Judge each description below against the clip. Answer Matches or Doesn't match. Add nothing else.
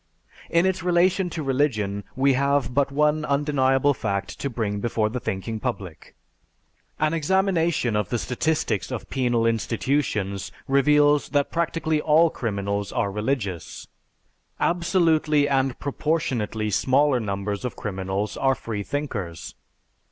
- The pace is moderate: Doesn't match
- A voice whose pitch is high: Doesn't match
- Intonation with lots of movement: Matches